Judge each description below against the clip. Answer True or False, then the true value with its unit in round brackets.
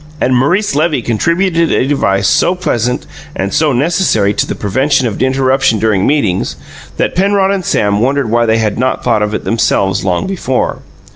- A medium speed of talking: True (180 wpm)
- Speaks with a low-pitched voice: True (130 Hz)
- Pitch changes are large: True (6.7 semitones)